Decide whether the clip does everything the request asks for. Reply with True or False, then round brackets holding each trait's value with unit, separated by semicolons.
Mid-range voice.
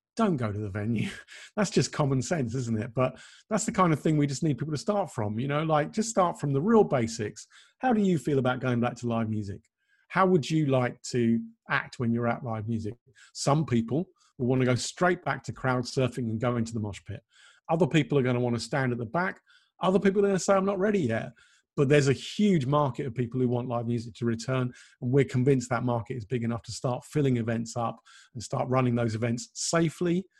False (130 Hz)